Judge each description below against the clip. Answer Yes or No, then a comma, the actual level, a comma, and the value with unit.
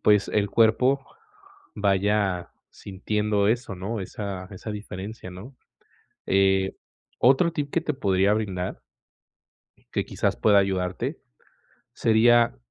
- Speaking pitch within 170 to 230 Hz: No, low, 105 Hz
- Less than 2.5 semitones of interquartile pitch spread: No, average, 2.9 semitones